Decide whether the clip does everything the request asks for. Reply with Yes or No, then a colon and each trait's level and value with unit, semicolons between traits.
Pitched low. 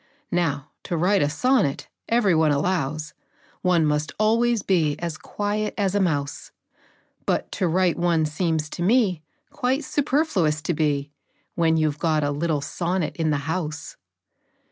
No: medium, 165 Hz